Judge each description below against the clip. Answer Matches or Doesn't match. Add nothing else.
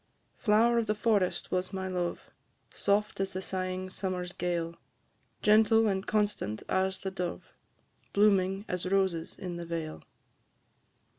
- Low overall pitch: Doesn't match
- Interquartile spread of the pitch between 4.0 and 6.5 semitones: Doesn't match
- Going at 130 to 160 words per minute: Matches